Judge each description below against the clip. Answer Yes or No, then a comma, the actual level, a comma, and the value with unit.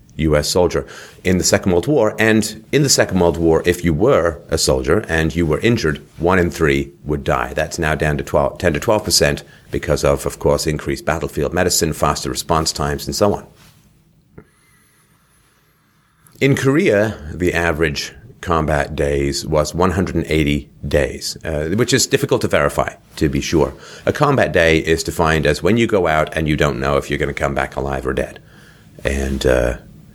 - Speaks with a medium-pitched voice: No, very low, 80 Hz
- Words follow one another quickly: No, average, 195 wpm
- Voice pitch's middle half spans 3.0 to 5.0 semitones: Yes, average, 3.6 semitones